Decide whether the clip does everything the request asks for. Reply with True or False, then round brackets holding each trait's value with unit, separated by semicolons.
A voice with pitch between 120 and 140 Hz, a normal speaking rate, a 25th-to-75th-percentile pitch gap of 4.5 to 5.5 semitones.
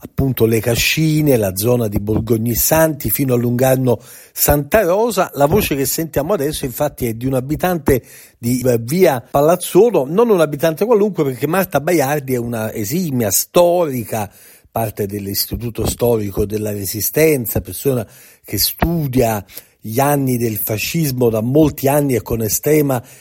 True (130 Hz; 140 wpm; 5.0 semitones)